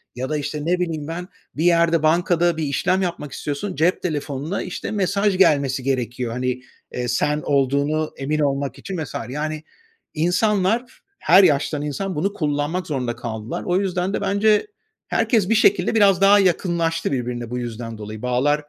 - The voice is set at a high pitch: No, medium, 155 Hz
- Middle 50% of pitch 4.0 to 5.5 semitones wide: Yes, average, 4.9 semitones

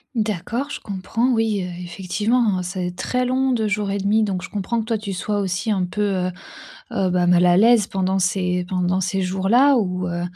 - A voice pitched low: No, high, 195 Hz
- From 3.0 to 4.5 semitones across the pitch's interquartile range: Yes, average, 3.4 semitones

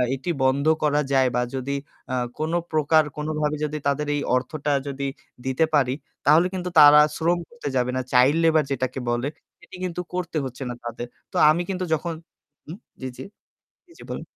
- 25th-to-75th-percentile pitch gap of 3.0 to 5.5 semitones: Yes, average, 3.7 semitones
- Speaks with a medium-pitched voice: Yes, medium, 150 Hz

